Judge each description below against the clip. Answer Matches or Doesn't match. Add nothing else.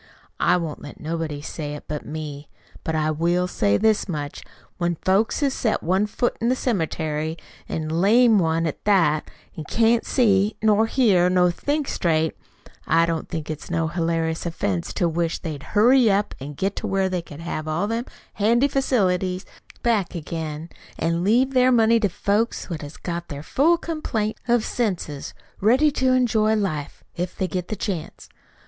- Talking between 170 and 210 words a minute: Matches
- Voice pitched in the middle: Matches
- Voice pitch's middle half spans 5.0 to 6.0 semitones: Matches